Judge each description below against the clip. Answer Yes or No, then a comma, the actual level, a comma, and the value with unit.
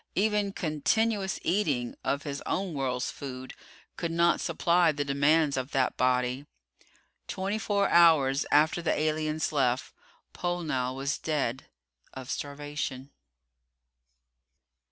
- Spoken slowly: Yes, slow, 115 wpm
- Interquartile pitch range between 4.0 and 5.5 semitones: Yes, average, 4.3 semitones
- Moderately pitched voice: Yes, medium, 150 Hz